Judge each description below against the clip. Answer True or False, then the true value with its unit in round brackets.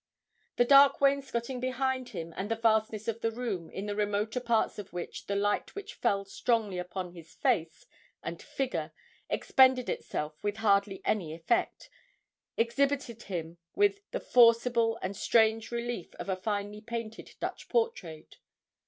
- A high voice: True (220 Hz)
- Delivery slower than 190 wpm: True (150 wpm)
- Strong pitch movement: False (3.7 semitones)